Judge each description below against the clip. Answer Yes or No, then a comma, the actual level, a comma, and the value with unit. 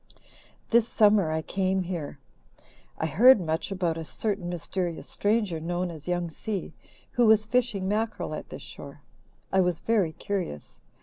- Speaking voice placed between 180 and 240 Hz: Yes, medium, 185 Hz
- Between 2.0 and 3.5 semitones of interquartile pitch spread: No, average, 4.2 semitones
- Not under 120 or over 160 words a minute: Yes, average, 150 wpm